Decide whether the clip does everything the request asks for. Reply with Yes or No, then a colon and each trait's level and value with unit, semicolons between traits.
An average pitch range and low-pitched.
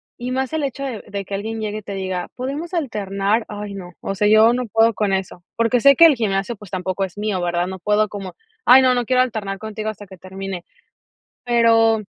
No: average, 3.6 semitones; high, 215 Hz